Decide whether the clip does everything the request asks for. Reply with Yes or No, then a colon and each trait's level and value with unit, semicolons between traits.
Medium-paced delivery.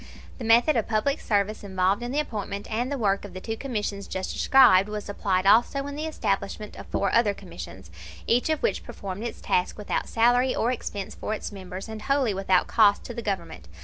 No: fast, 210 wpm